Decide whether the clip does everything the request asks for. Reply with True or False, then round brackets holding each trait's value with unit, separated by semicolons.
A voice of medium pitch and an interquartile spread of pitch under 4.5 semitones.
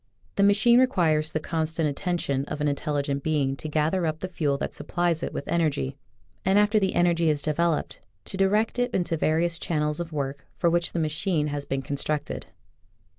True (160 Hz; 2.9 semitones)